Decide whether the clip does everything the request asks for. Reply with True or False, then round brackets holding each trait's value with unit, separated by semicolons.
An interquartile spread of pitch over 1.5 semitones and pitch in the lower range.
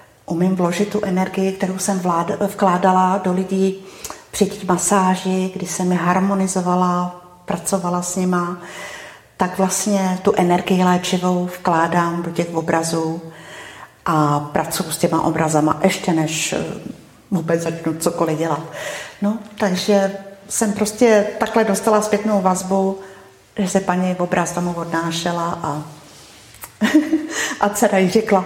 False (2.5 semitones; 185 Hz)